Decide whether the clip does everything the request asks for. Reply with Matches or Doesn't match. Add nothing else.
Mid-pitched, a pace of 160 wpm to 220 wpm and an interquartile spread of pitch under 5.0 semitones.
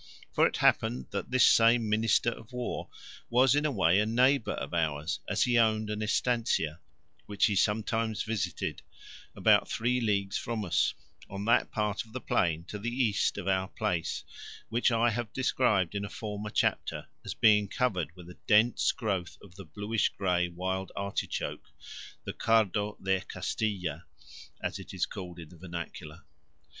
Doesn't match